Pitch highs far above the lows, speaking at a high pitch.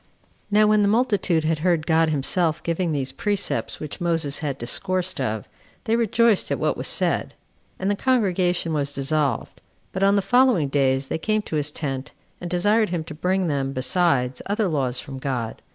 No: wide, 5.9 semitones; medium, 165 Hz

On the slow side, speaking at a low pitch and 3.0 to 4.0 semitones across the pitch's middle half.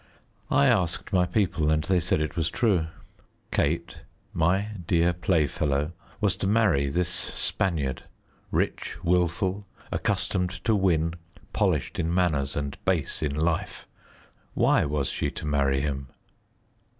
Yes: slow, 130 wpm; very low, 85 Hz; average, 3.6 semitones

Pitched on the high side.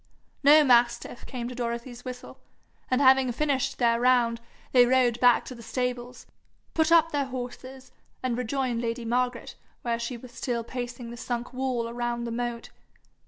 Yes: high, 245 Hz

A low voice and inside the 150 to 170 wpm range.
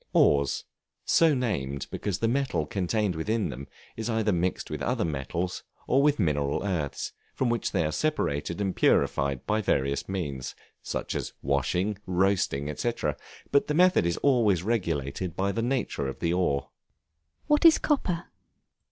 Yes: very low, 95 Hz; average, 155 wpm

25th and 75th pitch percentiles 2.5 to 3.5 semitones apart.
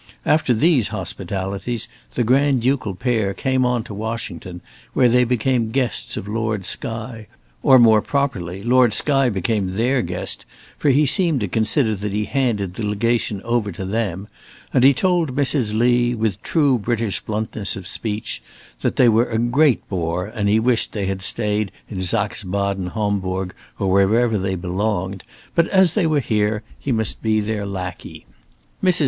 No: average, 3.9 semitones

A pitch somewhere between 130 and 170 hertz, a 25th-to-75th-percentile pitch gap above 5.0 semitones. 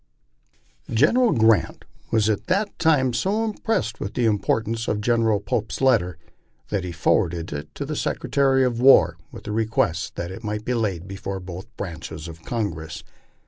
No: low, 110 Hz; wide, 5.5 semitones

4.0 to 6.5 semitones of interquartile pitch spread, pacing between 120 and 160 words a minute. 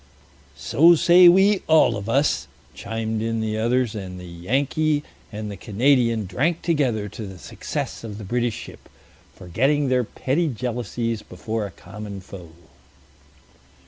Yes: average, 5.3 semitones; average, 145 wpm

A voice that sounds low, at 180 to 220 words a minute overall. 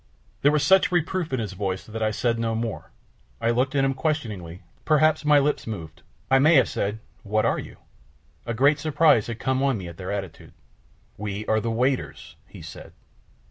Yes: low, 115 Hz; average, 195 wpm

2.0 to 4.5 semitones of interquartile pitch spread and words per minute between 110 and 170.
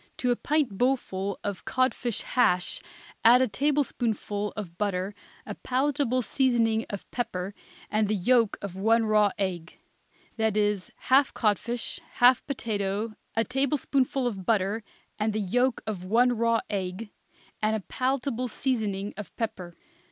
Yes: average, 3.8 semitones; average, 140 wpm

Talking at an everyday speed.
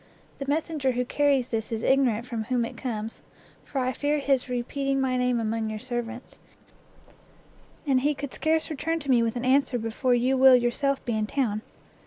Yes: average, 190 wpm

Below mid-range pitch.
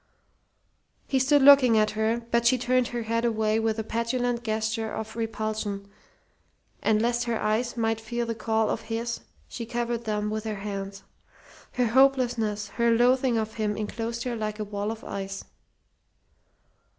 No: high, 225 Hz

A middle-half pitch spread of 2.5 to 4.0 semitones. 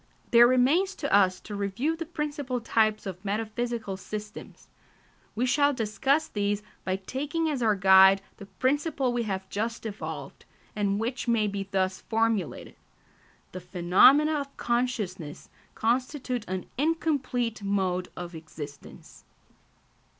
No: average, 5.0 semitones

